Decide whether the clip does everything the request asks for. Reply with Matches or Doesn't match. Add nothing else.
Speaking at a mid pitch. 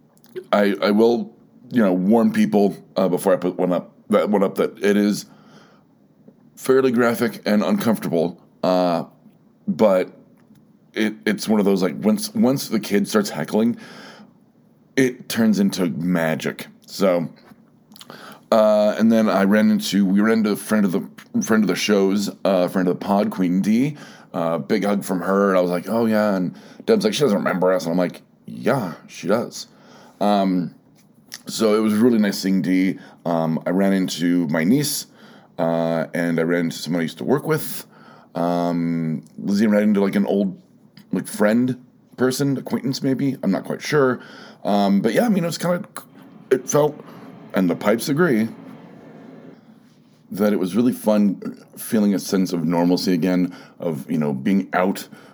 Doesn't match